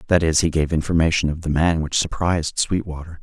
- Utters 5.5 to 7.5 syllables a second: Yes, 5.9 syllables/s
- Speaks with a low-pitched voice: Yes, very low, 80 Hz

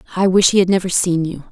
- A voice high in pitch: No, medium, 180 Hz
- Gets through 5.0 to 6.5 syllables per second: No, 6.9 syllables/s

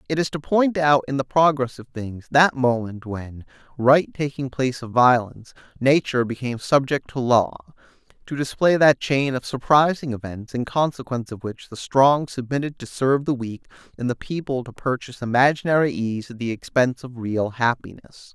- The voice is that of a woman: No, male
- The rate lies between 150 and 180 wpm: Yes, average, 175 wpm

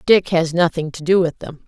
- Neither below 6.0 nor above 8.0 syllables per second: No, 5.2 syllables/s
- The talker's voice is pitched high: No, medium, 170 Hz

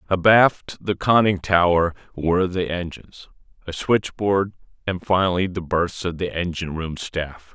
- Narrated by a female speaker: No, male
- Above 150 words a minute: No, average, 145 wpm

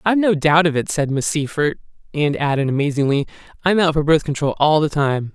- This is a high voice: No, medium, 150 Hz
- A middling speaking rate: No, fast, 215 wpm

